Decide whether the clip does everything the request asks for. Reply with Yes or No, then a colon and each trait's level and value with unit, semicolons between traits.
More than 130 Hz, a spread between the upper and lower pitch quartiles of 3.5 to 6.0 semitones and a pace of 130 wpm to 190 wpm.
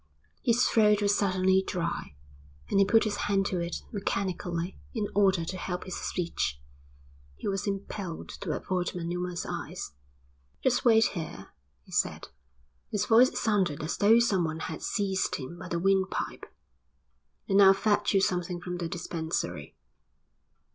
No: high, 190 Hz; average, 3.0 semitones; average, 150 wpm